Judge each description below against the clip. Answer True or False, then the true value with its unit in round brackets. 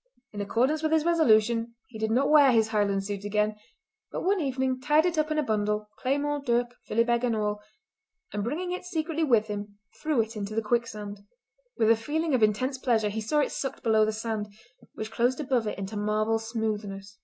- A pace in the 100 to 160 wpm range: False (205 wpm)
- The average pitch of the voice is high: True (230 Hz)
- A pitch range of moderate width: True (4.7 semitones)